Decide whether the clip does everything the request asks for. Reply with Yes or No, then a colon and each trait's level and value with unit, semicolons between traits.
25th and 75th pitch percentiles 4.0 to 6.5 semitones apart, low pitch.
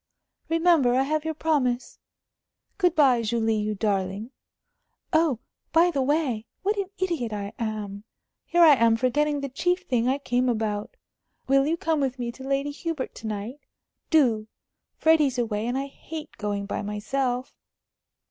No: wide, 5.6 semitones; very high, 260 Hz